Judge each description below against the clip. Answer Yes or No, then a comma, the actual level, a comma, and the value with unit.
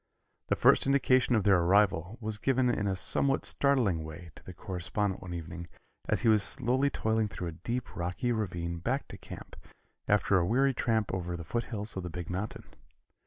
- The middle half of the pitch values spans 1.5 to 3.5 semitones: No, average, 5.2 semitones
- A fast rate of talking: No, average, 190 wpm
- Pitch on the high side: No, low, 105 Hz